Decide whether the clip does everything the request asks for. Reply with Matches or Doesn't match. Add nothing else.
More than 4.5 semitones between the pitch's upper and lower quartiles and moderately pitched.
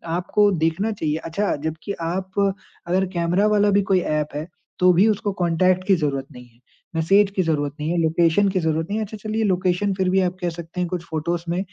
Doesn't match